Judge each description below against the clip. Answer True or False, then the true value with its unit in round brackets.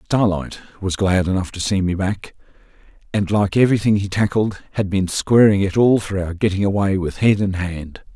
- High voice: False (100 Hz)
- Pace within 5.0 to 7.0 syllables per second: True (5.1 syllables/s)